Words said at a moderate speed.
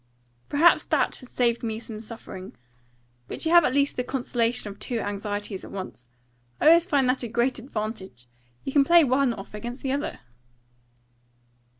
Yes: average, 175 wpm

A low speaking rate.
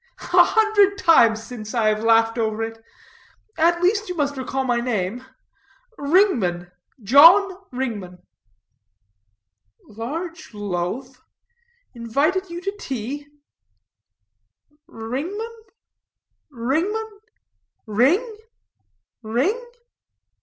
Yes: slow, 85 wpm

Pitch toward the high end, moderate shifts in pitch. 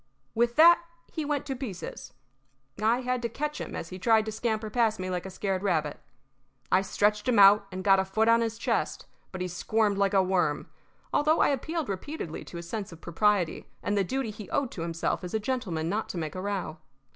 Yes: high, 205 Hz; average, 4.1 semitones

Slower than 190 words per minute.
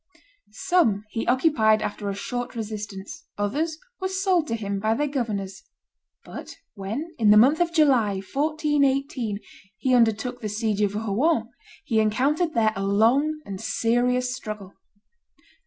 Yes: average, 140 wpm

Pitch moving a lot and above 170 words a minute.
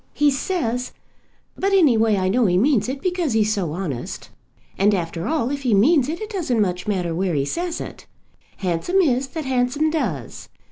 Yes: wide, 8.1 semitones; average, 190 wpm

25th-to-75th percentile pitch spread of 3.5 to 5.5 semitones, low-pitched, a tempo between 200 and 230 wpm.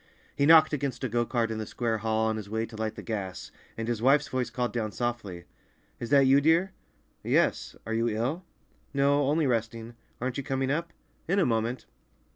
Yes: average, 3.8 semitones; low, 120 Hz; fast, 205 wpm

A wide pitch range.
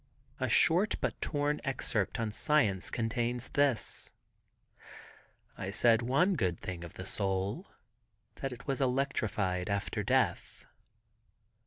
Yes: wide, 5.8 semitones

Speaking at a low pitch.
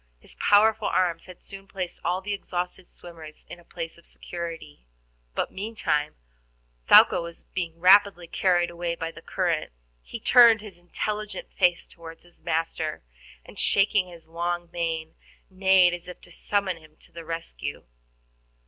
No: medium, 175 Hz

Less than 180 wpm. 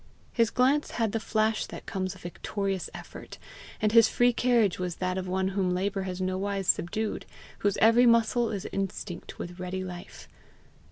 Yes: average, 170 wpm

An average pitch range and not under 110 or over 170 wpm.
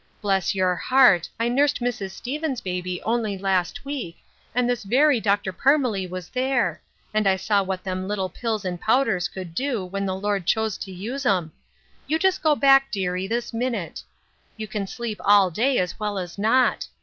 No: average, 4.9 semitones; average, 185 wpm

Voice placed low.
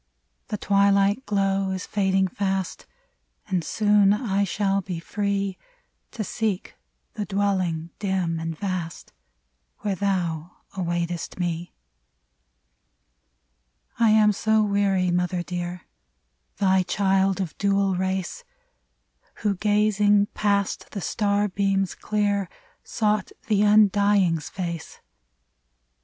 No: high, 195 Hz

